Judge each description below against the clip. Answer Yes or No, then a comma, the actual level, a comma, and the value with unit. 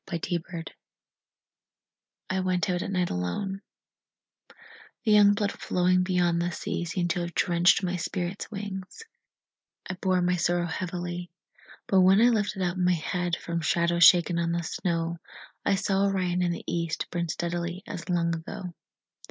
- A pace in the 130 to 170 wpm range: Yes, average, 160 wpm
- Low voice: No, medium, 175 Hz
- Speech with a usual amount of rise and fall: No, narrow, 1.6 semitones